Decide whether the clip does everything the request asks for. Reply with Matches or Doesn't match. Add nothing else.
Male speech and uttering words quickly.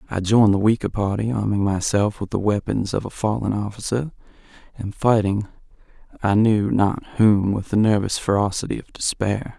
Doesn't match